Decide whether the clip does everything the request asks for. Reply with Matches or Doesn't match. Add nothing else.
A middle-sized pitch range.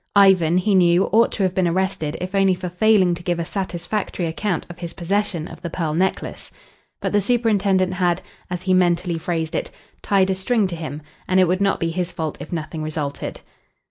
Doesn't match